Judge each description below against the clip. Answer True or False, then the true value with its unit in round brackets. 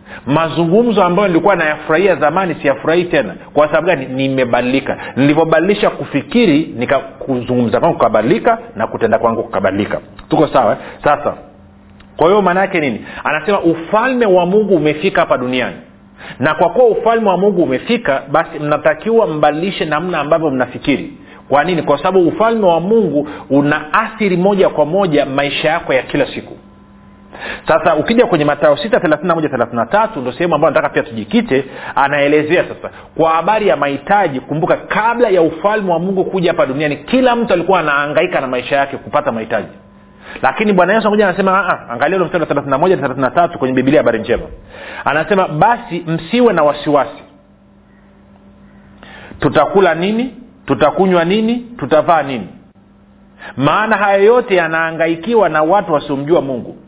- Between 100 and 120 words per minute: False (135 wpm)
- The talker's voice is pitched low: False (165 Hz)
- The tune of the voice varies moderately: False (5.8 semitones)